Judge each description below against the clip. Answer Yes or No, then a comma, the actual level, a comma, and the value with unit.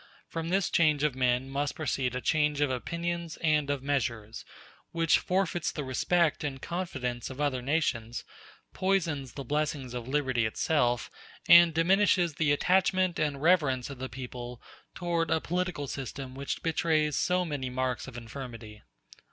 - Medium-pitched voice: Yes, medium, 145 Hz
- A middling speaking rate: Yes, average, 150 wpm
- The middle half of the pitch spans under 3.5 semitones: No, average, 4.4 semitones